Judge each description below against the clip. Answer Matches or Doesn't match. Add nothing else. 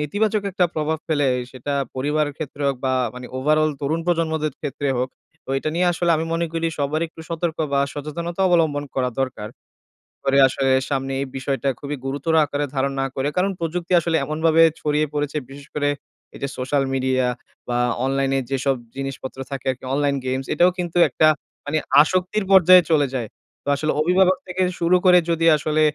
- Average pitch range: Matches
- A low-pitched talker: Doesn't match